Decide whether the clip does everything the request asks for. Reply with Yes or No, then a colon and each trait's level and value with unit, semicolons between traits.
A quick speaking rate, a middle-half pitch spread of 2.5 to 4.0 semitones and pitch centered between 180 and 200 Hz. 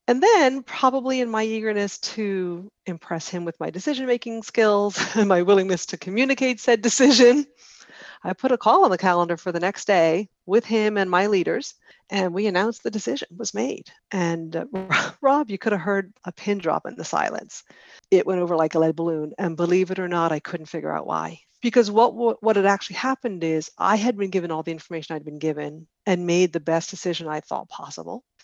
No: fast, 210 wpm; average, 4.9 semitones; high, 190 Hz